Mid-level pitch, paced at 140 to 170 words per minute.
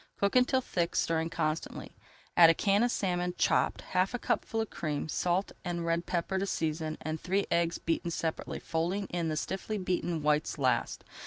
No: medium, 170 Hz; average, 180 wpm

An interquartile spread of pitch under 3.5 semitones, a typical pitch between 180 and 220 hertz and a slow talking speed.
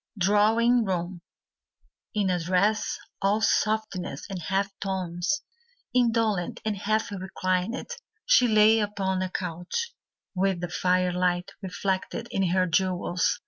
Yes: average, 3.0 semitones; high, 190 Hz; slow, 115 wpm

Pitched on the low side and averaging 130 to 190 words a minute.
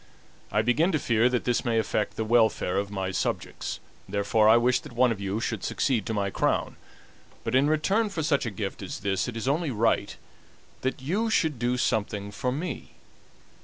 No: low, 120 Hz; average, 200 wpm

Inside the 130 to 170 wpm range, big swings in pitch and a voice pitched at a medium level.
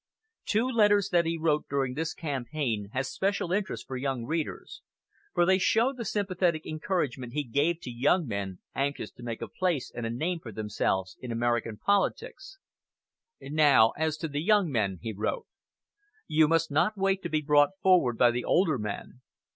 No: average, 180 wpm; wide, 6.9 semitones; medium, 150 Hz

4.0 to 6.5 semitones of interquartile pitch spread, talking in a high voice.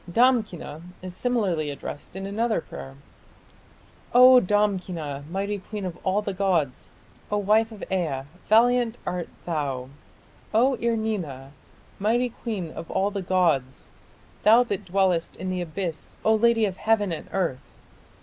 Yes: average, 4.8 semitones; high, 195 Hz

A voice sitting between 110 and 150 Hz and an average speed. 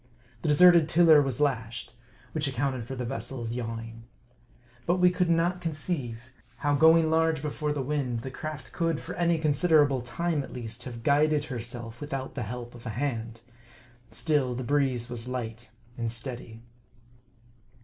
Yes: low, 135 Hz; average, 160 wpm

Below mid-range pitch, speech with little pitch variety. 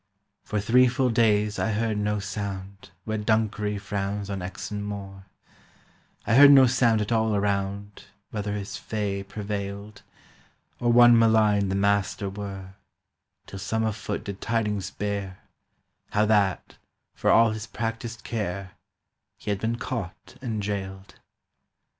Yes: low, 105 Hz; narrow, 2.0 semitones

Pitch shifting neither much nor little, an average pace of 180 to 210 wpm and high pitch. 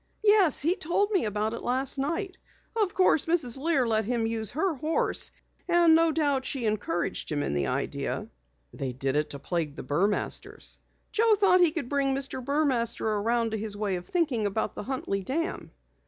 No: wide, 7.6 semitones; average, 185 wpm; very high, 260 Hz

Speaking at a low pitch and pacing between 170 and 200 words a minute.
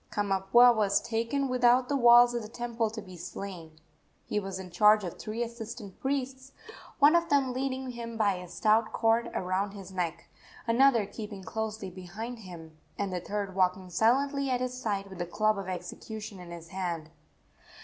No: high, 215 Hz; average, 180 wpm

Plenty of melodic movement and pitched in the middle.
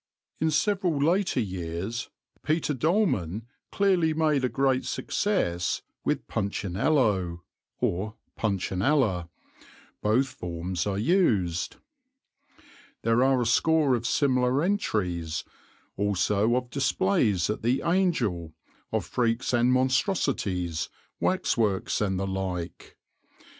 No: wide, 7.7 semitones; low, 115 Hz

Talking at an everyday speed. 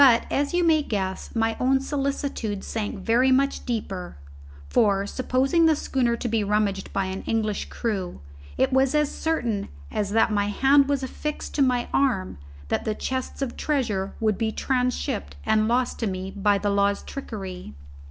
Yes: average, 170 wpm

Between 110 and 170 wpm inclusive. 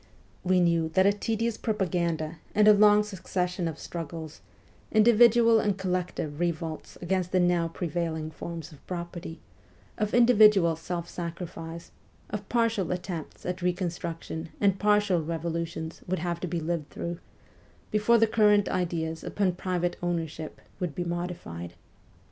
Yes: slow, 135 wpm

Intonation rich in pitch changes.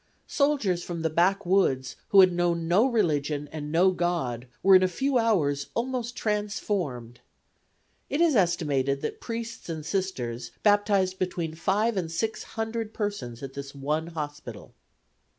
Yes: wide, 5.9 semitones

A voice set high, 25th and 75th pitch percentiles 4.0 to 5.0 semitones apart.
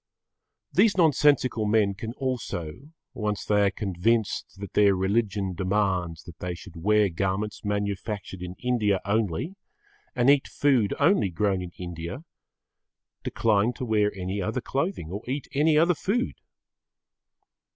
No: low, 105 Hz; average, 4.7 semitones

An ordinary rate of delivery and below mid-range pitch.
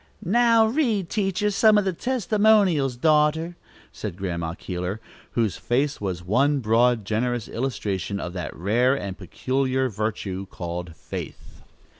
No: slow, 130 wpm; low, 125 Hz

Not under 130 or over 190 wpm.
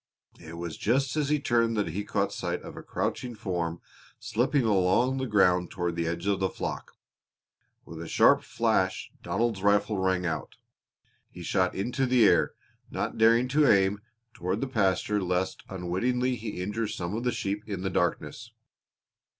Yes: average, 170 wpm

